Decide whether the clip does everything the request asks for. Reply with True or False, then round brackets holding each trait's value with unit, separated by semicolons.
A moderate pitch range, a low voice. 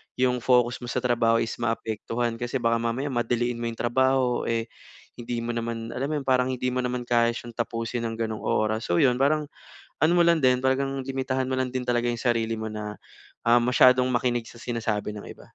False (1.7 semitones; 120 Hz)